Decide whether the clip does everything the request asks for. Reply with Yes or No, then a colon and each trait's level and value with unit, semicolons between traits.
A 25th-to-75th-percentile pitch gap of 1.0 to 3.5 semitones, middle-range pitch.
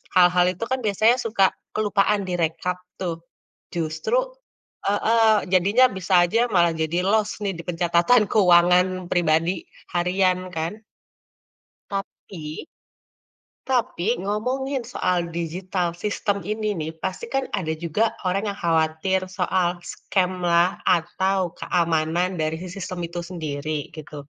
Yes: average, 3.1 semitones; medium, 180 Hz